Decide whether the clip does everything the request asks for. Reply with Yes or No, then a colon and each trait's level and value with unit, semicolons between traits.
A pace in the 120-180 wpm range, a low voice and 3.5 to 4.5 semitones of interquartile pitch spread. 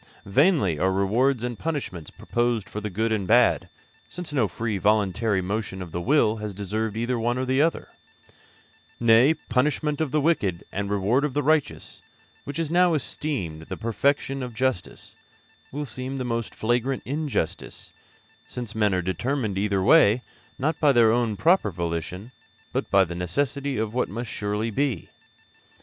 No: average, 170 wpm; low, 115 Hz; average, 5.3 semitones